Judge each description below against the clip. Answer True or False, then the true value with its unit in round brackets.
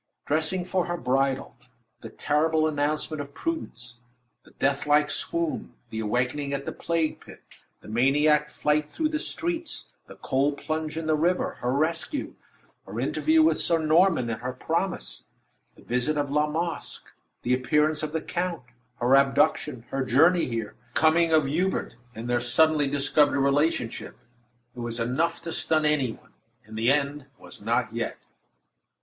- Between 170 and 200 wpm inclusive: False (160 wpm)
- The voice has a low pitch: False (150 Hz)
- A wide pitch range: False (3.5 semitones)